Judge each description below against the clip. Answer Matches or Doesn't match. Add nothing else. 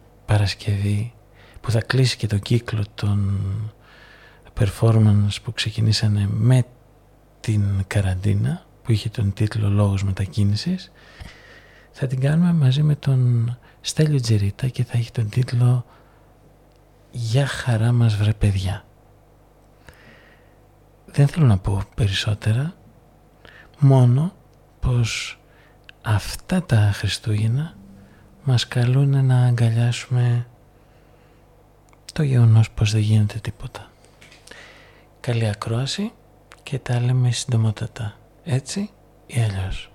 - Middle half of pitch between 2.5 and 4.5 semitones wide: Matches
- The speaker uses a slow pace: Matches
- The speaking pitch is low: Matches